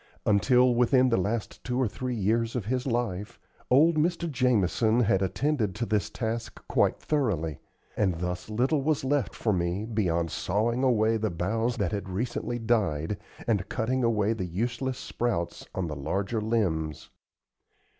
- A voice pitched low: Yes, low, 110 Hz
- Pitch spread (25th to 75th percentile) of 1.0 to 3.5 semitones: No, average, 4.3 semitones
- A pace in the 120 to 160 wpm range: Yes, average, 155 wpm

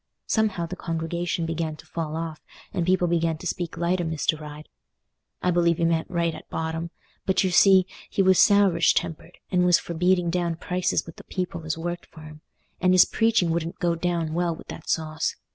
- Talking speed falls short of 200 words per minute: No, fast, 205 wpm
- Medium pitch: Yes, medium, 170 Hz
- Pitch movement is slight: Yes, narrow, 1.6 semitones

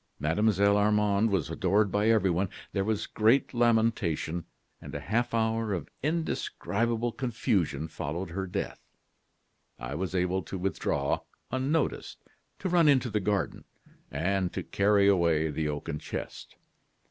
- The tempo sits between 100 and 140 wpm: Yes, slow, 135 wpm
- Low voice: Yes, low, 100 Hz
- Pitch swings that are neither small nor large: Yes, average, 4.4 semitones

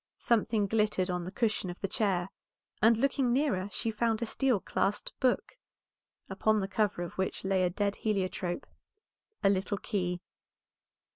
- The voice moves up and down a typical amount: Yes, average, 3.2 semitones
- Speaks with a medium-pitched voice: No, high, 205 Hz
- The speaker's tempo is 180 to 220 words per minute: No, average, 155 wpm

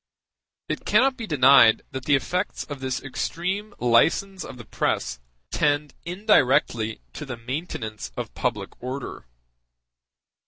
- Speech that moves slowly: Yes, slow, 125 wpm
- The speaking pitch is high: No, medium, 140 Hz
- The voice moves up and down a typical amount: No, wide, 6.4 semitones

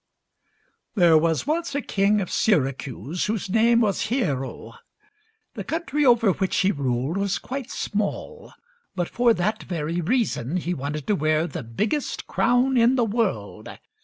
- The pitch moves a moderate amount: No, wide, 7.3 semitones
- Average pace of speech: Yes, average, 150 wpm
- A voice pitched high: Yes, high, 200 Hz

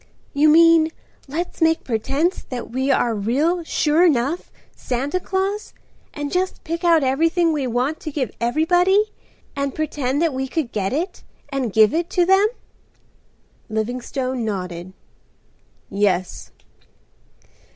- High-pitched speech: Yes, very high, 290 Hz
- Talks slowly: Yes, slow, 130 wpm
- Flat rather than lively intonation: No, wide, 5.5 semitones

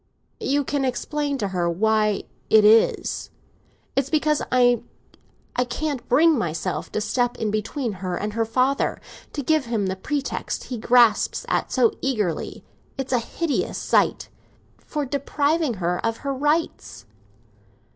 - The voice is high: Yes, high, 245 Hz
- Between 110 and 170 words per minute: Yes, slow, 135 wpm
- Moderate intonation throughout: Yes, average, 5.0 semitones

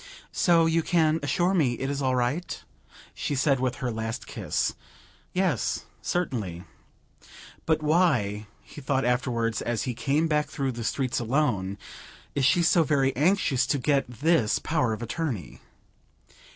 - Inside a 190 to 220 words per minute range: No, average, 150 wpm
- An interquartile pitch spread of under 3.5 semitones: No, average, 4.7 semitones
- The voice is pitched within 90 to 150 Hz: Yes, low, 135 Hz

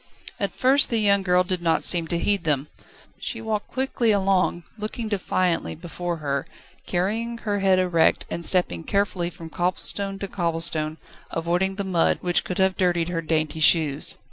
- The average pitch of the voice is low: No, medium, 180 Hz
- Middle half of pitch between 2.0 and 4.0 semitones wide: Yes, average, 3.1 semitones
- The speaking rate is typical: Yes, average, 170 wpm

